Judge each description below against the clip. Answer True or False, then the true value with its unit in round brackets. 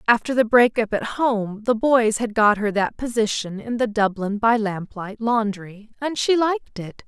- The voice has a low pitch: False (225 Hz)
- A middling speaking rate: True (185 wpm)